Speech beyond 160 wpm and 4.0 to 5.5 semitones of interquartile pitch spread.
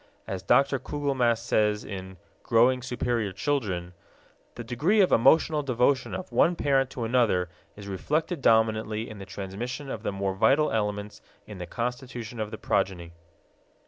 No: average, 150 wpm; average, 4.7 semitones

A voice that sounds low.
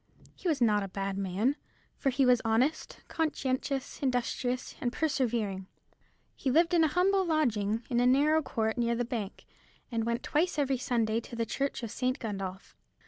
No: high, 245 Hz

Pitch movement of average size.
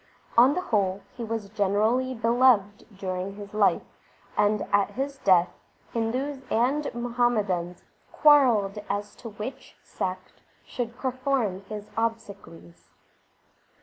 Yes: average, 3.8 semitones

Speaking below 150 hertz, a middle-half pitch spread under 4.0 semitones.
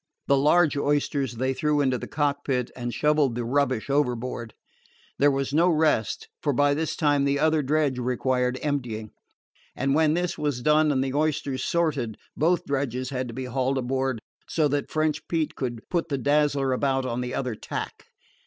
Yes: medium, 140 Hz; average, 2.9 semitones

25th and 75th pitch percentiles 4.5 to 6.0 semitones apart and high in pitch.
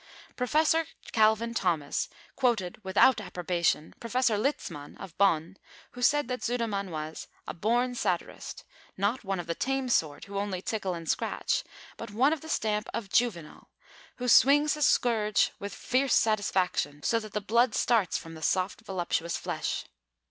Yes: average, 5.3 semitones; high, 210 Hz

